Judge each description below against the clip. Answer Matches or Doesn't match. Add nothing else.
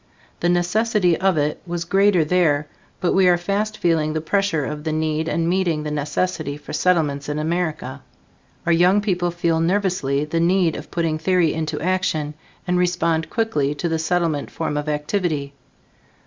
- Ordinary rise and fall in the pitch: Matches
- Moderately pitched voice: Matches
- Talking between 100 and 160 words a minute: Doesn't match